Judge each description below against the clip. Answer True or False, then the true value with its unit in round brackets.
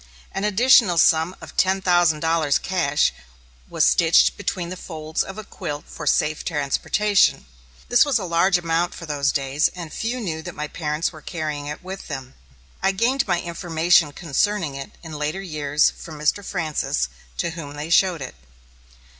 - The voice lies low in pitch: False (165 Hz)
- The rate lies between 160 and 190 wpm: True (170 wpm)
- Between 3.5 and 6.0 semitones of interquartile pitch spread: True (3.8 semitones)